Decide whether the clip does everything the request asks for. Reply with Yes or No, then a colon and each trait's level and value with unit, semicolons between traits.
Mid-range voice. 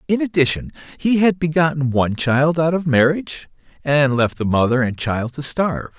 Yes: medium, 145 Hz